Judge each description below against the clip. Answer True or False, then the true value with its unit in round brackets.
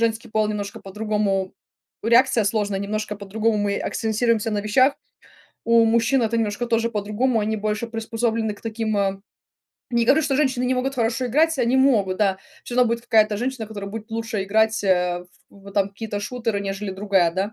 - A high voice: True (220 Hz)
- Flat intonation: True (2.3 semitones)